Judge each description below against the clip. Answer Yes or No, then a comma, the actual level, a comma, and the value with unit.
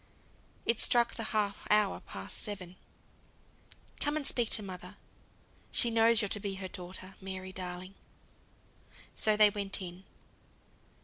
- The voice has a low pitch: No, high, 200 Hz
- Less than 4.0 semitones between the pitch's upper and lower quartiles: Yes, narrow, 2.6 semitones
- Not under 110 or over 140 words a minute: Yes, slow, 135 wpm